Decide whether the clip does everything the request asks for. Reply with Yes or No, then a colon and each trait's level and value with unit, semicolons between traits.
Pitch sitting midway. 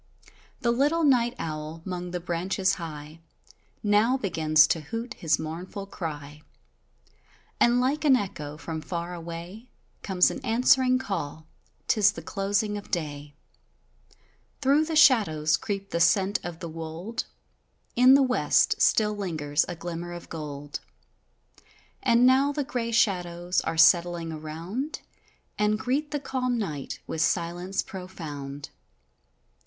Yes: medium, 180 Hz